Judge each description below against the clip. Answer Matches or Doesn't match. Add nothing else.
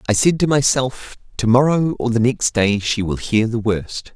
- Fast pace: Matches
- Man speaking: Matches